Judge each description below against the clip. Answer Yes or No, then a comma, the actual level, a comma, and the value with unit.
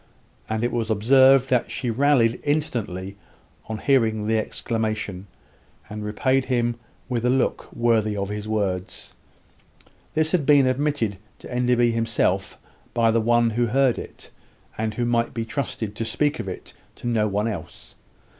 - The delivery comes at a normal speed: Yes, average, 155 wpm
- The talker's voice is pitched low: Yes, low, 115 Hz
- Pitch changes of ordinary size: Yes, average, 3.0 semitones